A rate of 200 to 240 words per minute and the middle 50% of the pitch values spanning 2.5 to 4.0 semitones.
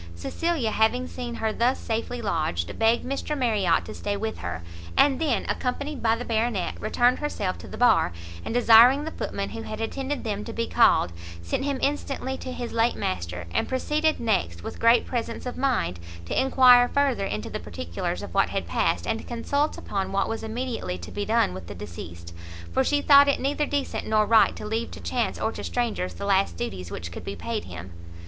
No: fast, 205 wpm; average, 5.2 semitones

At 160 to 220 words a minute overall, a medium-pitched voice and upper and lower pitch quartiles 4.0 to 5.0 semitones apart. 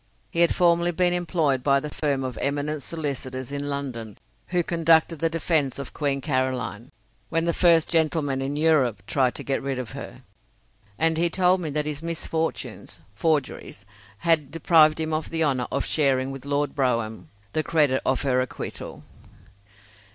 No: average, 165 wpm; medium, 145 Hz; average, 3.6 semitones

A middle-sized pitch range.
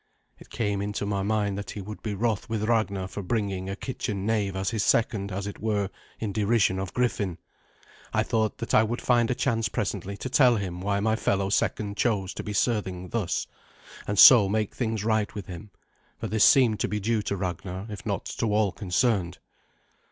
No: narrow, 2.2 semitones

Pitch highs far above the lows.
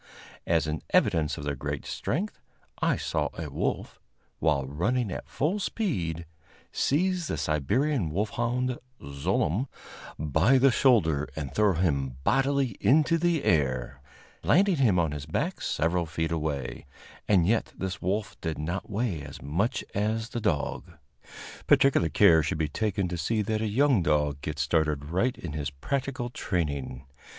Yes: wide, 8.3 semitones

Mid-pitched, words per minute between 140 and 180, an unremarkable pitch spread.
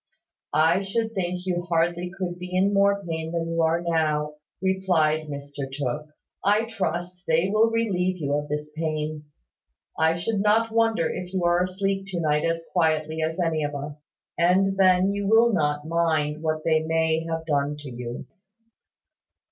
Yes: medium, 165 Hz; average, 170 wpm; average, 3.5 semitones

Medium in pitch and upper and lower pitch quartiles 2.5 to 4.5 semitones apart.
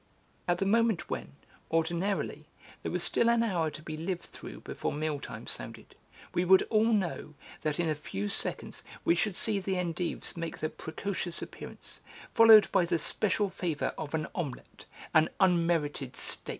Yes: medium, 170 Hz; average, 3.8 semitones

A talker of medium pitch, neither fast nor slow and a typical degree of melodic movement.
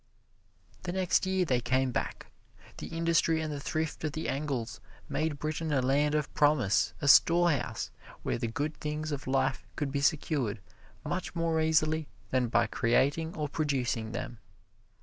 Yes: medium, 150 Hz; average, 160 wpm; average, 3.3 semitones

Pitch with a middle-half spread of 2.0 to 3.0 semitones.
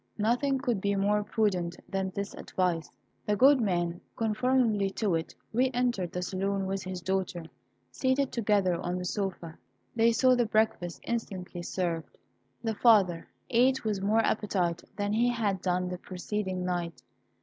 No: average, 3.8 semitones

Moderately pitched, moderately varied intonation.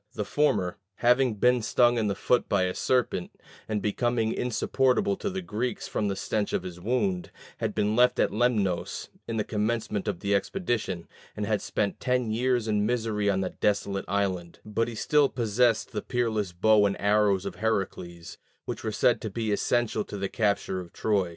No: low, 105 Hz; average, 3.2 semitones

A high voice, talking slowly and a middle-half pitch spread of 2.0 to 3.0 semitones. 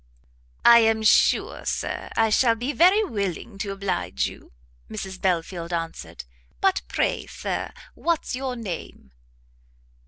No: high, 215 Hz; slow, 125 wpm; wide, 5.5 semitones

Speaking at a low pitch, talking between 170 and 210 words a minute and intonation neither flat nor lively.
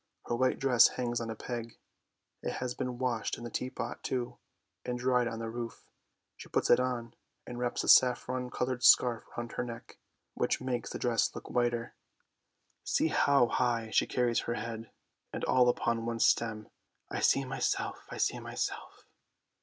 No: low, 120 Hz; average, 175 wpm; narrow, 1.3 semitones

